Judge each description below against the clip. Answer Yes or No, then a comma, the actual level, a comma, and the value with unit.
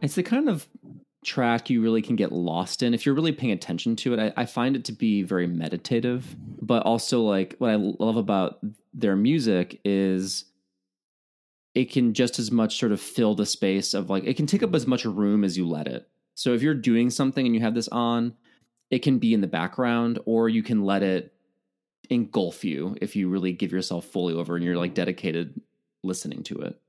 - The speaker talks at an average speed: No, fast, 215 wpm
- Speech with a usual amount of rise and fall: Yes, average, 4.5 semitones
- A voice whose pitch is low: Yes, low, 110 Hz